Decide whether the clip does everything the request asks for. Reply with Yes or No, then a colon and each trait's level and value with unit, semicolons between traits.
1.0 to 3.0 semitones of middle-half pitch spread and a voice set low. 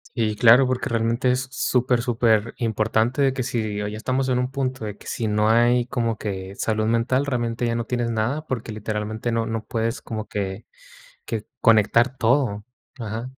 Yes: narrow, 2.4 semitones; low, 115 Hz